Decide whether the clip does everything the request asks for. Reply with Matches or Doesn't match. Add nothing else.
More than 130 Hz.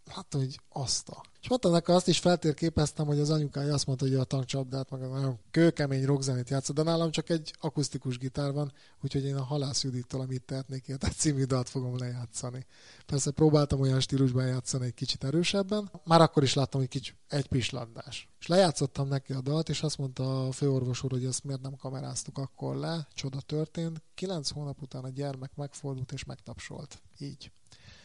Matches